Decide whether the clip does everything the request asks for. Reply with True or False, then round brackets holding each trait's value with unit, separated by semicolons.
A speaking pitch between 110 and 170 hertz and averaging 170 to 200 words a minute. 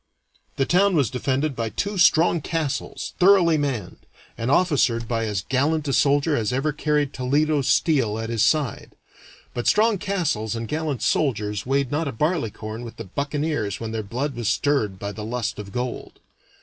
True (135 Hz; 175 wpm)